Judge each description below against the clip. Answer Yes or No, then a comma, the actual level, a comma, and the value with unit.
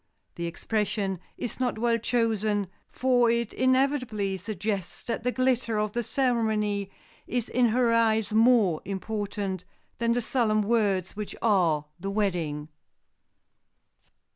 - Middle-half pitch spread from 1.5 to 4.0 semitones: Yes, average, 3.1 semitones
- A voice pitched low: No, high, 220 Hz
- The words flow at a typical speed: No, slow, 125 wpm